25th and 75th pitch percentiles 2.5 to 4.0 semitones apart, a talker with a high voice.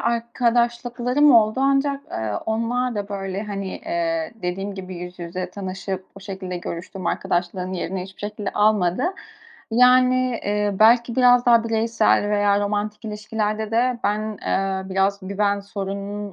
Yes: average, 3.4 semitones; high, 205 Hz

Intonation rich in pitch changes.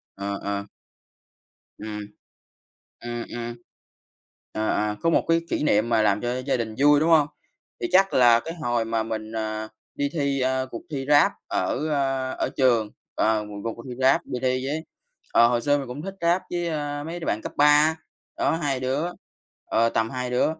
No: average, 4.5 semitones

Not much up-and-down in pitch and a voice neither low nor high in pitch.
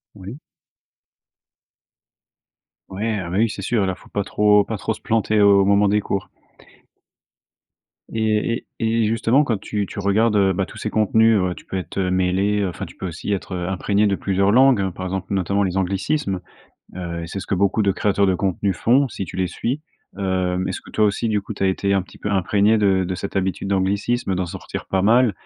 No: narrow, 2.2 semitones; low, 100 Hz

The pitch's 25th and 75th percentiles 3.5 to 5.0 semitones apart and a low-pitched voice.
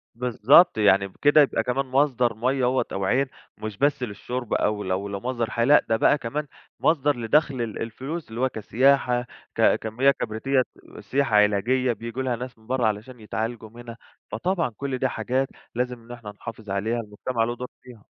No: average, 3.1 semitones; low, 120 Hz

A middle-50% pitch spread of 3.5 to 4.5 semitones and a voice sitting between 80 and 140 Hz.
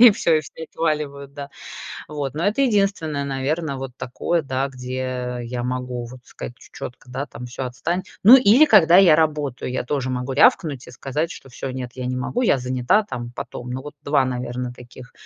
Yes: average, 4.0 semitones; low, 135 Hz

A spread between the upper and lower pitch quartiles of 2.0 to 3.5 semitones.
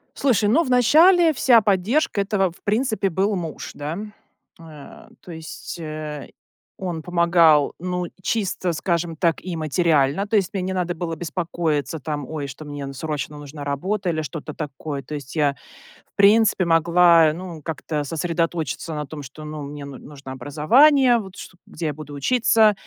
No: average, 4.4 semitones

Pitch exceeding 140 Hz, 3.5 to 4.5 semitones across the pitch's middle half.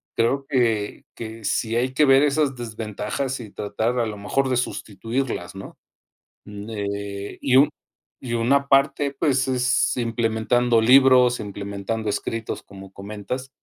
No: low, 115 Hz; average, 4.1 semitones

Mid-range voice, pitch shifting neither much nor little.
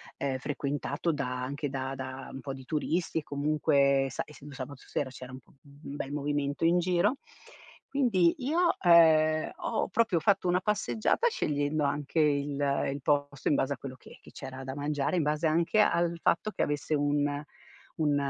Yes: medium, 145 Hz; average, 3.2 semitones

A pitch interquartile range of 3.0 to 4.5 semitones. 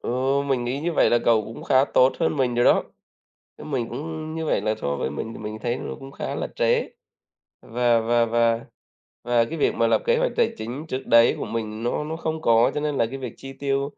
Yes: average, 3.8 semitones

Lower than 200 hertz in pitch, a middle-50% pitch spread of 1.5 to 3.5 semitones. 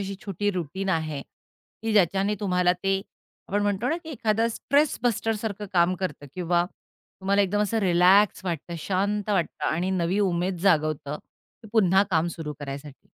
Yes: high, 190 Hz; average, 3.1 semitones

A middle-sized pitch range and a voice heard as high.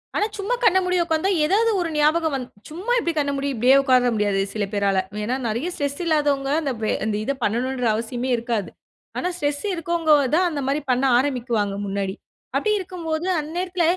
No: wide, 5.9 semitones; very high, 285 Hz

